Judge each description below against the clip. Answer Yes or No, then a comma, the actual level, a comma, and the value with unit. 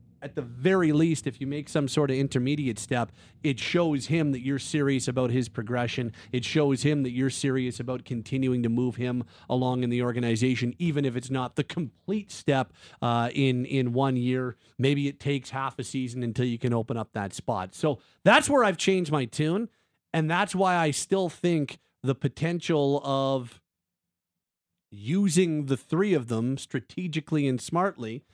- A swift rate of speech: No, average, 180 wpm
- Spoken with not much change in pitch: No, average, 3.7 semitones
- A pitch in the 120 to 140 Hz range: Yes, low, 135 Hz